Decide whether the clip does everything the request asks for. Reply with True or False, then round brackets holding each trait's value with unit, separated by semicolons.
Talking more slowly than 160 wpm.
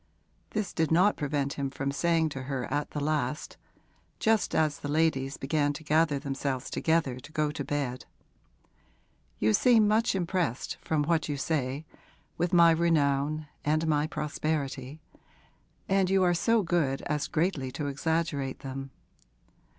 True (150 wpm)